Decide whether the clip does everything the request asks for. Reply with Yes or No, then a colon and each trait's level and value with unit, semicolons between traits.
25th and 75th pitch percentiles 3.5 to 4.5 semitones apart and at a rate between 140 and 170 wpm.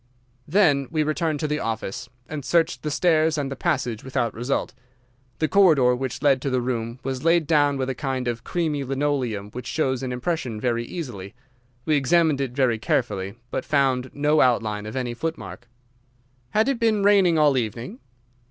No: average, 4.2 semitones; average, 180 wpm